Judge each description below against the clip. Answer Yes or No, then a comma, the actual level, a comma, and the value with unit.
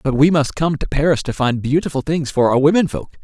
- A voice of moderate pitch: Yes, medium, 145 Hz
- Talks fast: Yes, fast, 260 wpm